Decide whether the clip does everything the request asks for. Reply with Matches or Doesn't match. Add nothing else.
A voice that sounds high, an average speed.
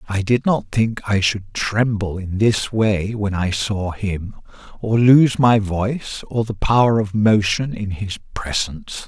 Doesn't match